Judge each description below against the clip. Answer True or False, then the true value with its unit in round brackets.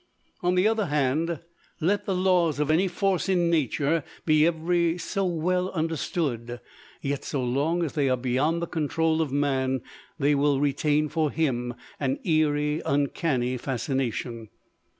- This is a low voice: False (155 Hz)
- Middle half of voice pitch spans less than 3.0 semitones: False (3.8 semitones)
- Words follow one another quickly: False (150 wpm)